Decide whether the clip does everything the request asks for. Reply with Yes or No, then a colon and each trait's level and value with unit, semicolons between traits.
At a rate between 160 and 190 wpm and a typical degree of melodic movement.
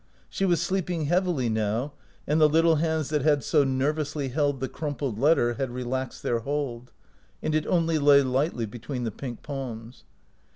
Yes: average, 175 wpm; average, 3.8 semitones